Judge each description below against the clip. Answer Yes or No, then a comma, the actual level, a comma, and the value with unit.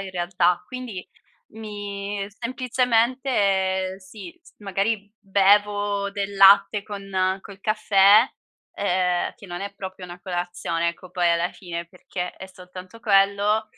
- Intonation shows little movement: Yes, narrow, 2.0 semitones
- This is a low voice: No, high, 195 Hz